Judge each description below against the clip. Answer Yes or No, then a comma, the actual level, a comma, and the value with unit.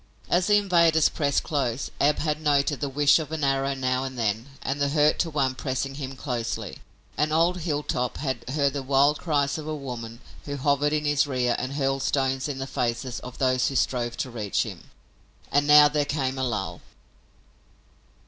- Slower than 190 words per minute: No, average, 195 wpm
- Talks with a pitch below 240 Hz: Yes, medium, 140 Hz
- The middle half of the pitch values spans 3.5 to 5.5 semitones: No, narrow, 2.4 semitones